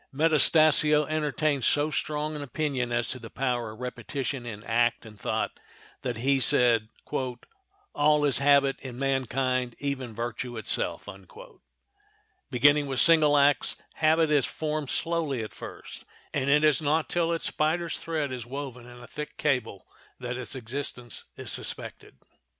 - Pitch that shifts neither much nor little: Yes, average, 3.6 semitones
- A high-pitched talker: No, medium, 140 Hz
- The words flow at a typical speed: Yes, average, 150 wpm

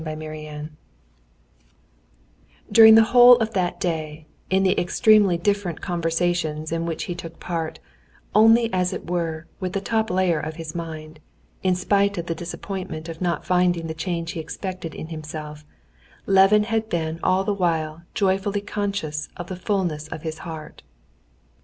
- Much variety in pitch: No, average, 3.5 semitones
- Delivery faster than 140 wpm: Yes, average, 160 wpm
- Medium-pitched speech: Yes, medium, 175 Hz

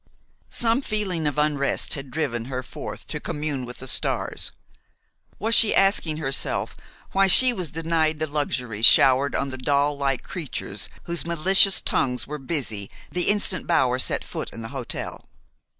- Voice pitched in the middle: Yes, medium, 150 Hz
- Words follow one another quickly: No, average, 160 wpm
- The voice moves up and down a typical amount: Yes, average, 4.6 semitones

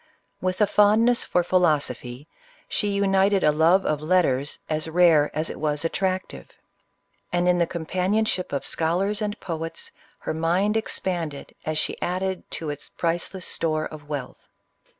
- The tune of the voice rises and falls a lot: No, average, 3.6 semitones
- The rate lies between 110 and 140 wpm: No, average, 155 wpm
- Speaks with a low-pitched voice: No, medium, 175 Hz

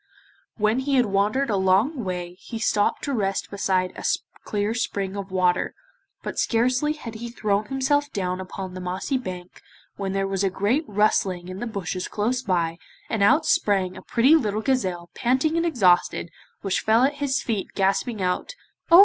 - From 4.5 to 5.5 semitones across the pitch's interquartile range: Yes, average, 5.0 semitones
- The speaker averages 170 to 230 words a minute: Yes, average, 180 wpm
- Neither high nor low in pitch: No, high, 205 Hz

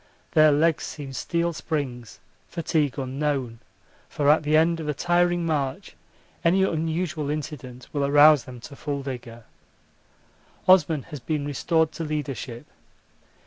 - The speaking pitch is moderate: Yes, medium, 150 Hz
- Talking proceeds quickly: No, slow, 135 wpm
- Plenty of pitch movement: No, average, 2.9 semitones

